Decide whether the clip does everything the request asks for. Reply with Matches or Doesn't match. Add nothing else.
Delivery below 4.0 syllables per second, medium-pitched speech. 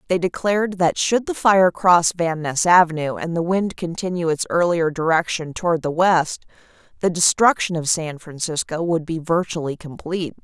Doesn't match